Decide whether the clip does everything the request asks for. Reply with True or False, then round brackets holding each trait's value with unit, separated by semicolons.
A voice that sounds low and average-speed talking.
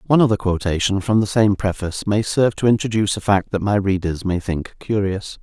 False (100 Hz; 210 wpm)